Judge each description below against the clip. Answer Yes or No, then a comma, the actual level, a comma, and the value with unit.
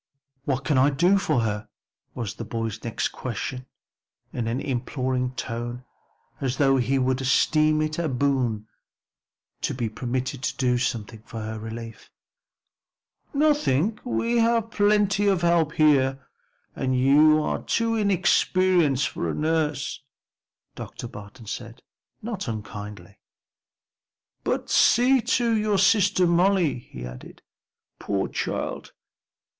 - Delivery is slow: Yes, slow, 125 wpm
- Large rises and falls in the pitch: Yes, wide, 7.5 semitones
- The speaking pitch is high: No, low, 135 Hz